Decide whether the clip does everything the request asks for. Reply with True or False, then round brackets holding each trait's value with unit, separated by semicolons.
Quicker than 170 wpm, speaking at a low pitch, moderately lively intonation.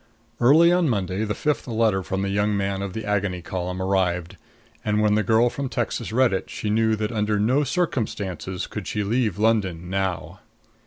True (190 wpm; 105 Hz; 3.1 semitones)